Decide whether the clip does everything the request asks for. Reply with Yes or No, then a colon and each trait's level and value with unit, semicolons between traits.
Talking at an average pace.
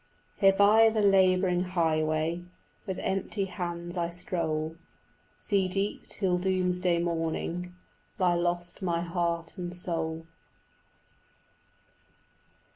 No: slow, 100 wpm